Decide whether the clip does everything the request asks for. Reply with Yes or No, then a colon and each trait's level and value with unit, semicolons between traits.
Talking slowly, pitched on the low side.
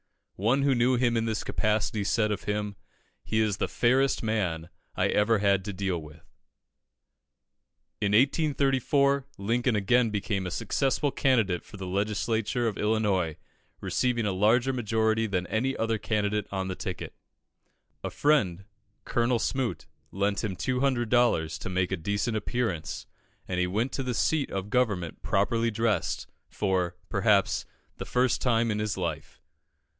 No: average, 150 wpm; low, 110 Hz